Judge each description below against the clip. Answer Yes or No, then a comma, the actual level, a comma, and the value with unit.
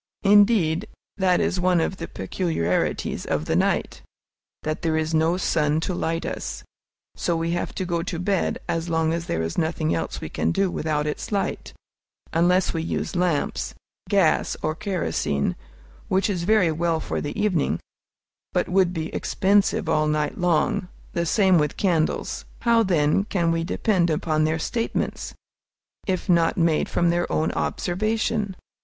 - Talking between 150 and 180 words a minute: Yes, average, 160 wpm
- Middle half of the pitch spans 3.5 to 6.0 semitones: No, average, 3.0 semitones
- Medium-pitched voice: Yes, medium, 170 Hz